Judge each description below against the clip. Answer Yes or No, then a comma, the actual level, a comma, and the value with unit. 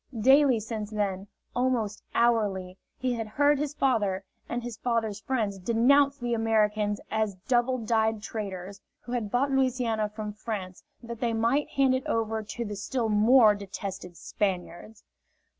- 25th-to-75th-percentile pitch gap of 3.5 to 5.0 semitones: No, average, 2.9 semitones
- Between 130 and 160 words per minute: Yes, average, 150 wpm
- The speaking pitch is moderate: No, high, 220 Hz